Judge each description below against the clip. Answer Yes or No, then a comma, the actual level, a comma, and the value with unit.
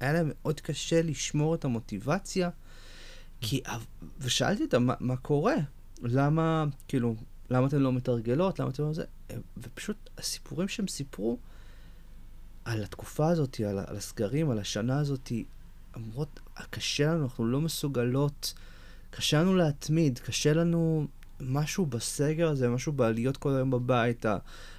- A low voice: Yes, low, 130 Hz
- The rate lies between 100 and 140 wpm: Yes, average, 130 wpm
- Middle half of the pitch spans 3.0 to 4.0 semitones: No, average, 5.2 semitones